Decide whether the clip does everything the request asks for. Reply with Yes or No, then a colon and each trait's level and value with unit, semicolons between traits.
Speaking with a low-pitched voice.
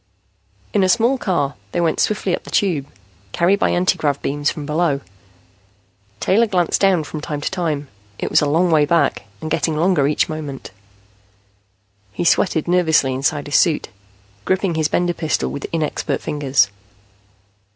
No: medium, 160 Hz